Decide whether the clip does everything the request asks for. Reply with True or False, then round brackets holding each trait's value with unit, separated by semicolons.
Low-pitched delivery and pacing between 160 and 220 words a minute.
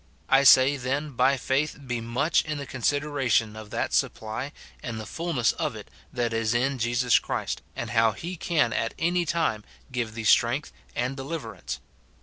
True (130 Hz; 170 wpm)